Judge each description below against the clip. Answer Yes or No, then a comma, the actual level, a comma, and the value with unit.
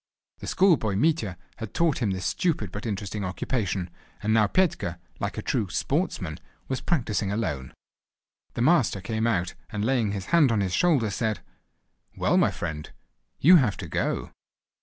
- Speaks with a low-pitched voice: Yes, low, 110 Hz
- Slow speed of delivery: No, average, 160 wpm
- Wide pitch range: Yes, wide, 5.8 semitones